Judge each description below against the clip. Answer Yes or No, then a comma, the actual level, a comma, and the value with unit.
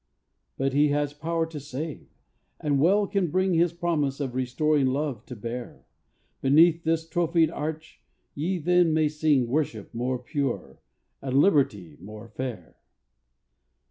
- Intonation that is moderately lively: Yes, average, 4.0 semitones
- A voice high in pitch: No, medium, 145 Hz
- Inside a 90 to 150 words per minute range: Yes, average, 140 wpm